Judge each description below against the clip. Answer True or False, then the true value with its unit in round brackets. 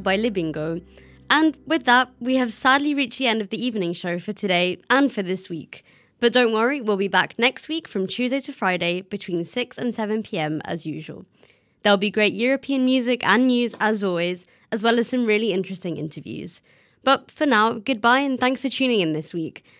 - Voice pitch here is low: False (220 Hz)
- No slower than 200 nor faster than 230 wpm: True (205 wpm)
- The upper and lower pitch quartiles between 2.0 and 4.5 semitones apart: False (5.5 semitones)